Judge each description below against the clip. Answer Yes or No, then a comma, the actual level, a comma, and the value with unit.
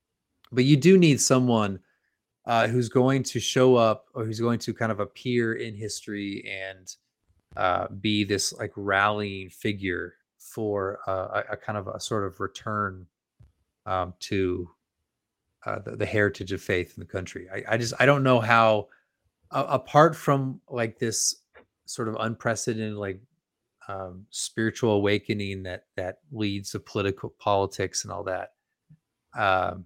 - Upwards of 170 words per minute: No, average, 155 wpm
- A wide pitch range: No, average, 3.4 semitones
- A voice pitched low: Yes, low, 105 Hz